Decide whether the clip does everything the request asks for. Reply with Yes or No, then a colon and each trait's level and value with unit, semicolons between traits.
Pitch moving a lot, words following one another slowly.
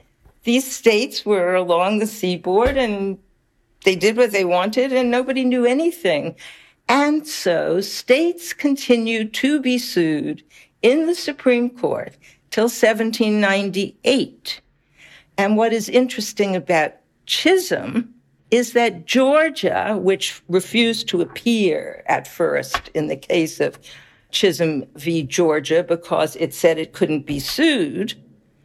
Yes: wide, 5.9 semitones; slow, 120 wpm